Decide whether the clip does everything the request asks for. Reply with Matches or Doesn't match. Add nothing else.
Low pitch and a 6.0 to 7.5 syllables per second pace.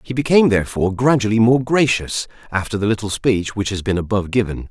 Matches